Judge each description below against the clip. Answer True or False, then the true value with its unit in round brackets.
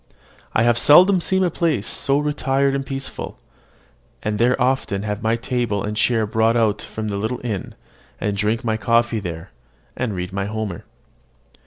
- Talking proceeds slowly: False (170 wpm)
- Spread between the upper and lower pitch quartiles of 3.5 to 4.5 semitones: True (4.1 semitones)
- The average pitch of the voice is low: True (115 Hz)